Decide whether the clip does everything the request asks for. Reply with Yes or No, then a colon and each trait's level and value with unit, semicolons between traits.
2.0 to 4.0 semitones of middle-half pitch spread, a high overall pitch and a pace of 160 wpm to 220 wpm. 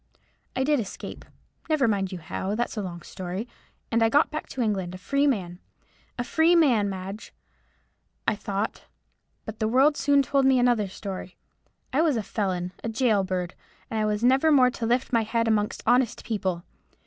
No: average, 5.0 semitones; high, 225 Hz; average, 180 wpm